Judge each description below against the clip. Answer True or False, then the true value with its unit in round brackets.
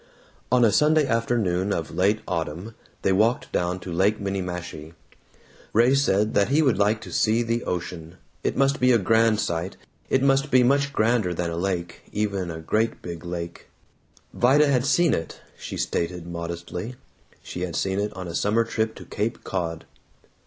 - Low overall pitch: True (100 Hz)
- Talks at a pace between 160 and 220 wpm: True (175 wpm)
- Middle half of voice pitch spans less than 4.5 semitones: False (5.2 semitones)